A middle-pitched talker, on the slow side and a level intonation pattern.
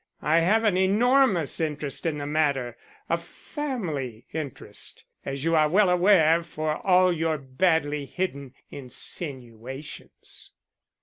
No: medium, 155 Hz; slow, 120 wpm; average, 4.3 semitones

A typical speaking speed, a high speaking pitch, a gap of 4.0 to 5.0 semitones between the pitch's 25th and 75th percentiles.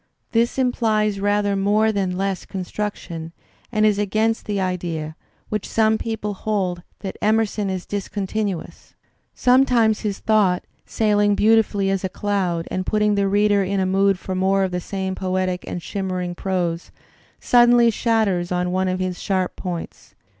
No: average, 155 wpm; high, 200 Hz; narrow, 2.5 semitones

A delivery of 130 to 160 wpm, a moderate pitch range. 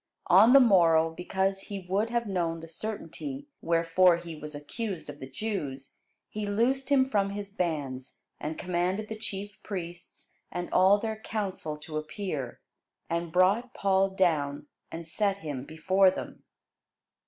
Yes: average, 150 wpm; average, 4.0 semitones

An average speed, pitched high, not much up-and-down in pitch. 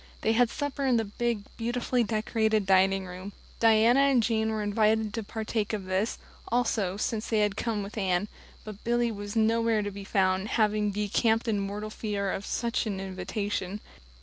Yes: average, 175 wpm; high, 215 Hz; narrow, 2.1 semitones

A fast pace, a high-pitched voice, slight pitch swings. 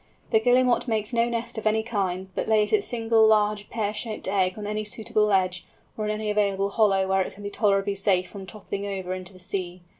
Yes: fast, 220 wpm; high, 210 Hz; narrow, 2.2 semitones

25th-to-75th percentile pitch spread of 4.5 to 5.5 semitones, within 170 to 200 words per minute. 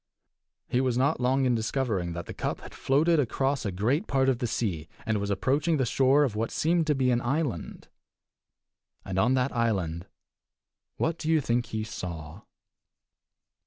Yes: average, 4.9 semitones; average, 175 wpm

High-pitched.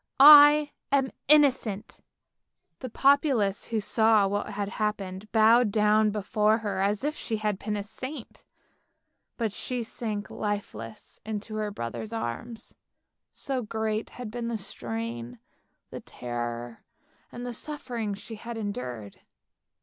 Yes: high, 215 Hz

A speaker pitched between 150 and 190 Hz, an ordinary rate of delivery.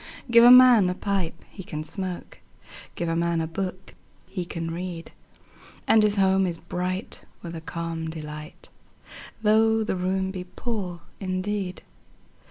Yes: medium, 185 Hz; average, 155 wpm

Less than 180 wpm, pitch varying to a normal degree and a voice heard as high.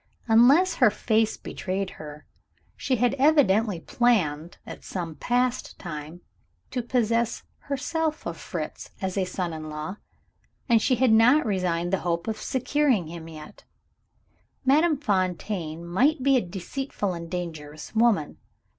No: slow, 135 wpm; wide, 6.6 semitones; high, 205 Hz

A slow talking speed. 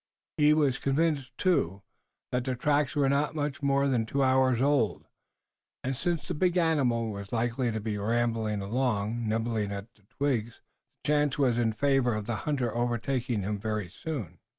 No: average, 175 wpm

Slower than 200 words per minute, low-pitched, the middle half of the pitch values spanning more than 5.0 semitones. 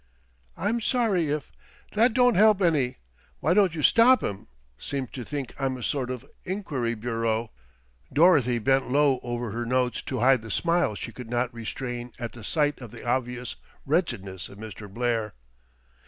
Yes: average, 170 wpm; low, 125 Hz; wide, 5.5 semitones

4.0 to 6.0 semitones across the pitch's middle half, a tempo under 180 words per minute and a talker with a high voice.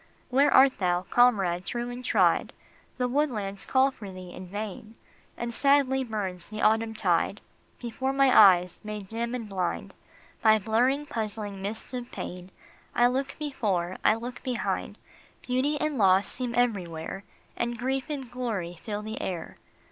Yes: average, 4.5 semitones; average, 155 wpm; high, 225 Hz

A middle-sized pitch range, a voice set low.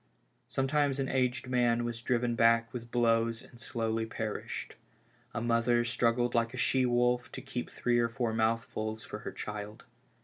No: narrow, 1.1 semitones; low, 120 Hz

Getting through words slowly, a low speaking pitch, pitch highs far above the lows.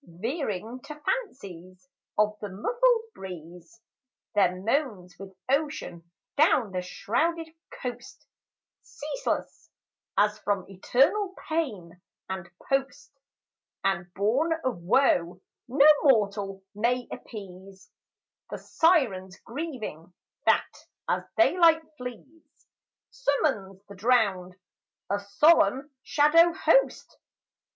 No: slow, 95 wpm; high, 220 Hz; wide, 7.7 semitones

